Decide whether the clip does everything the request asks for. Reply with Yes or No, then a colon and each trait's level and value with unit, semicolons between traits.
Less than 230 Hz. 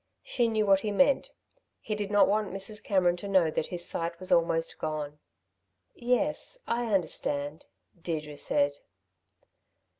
Yes: high, 190 Hz